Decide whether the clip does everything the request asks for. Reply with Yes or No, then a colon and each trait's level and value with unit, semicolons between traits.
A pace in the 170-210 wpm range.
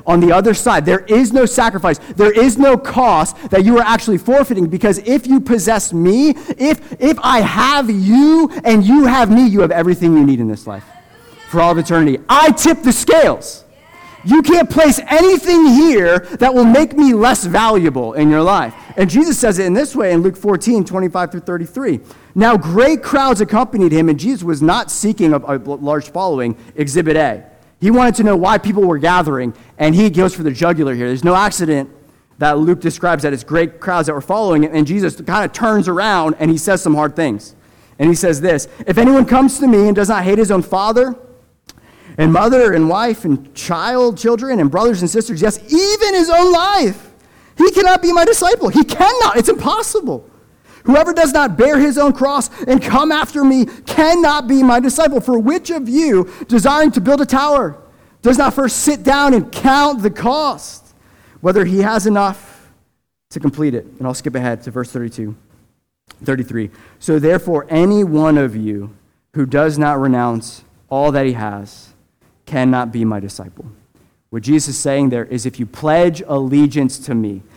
Yes: average, 195 wpm